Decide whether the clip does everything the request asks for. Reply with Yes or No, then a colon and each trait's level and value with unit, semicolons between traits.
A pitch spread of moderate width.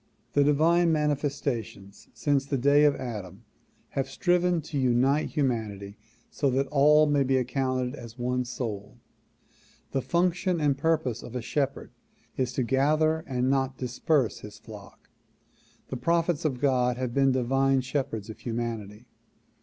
Yes: average, 3.3 semitones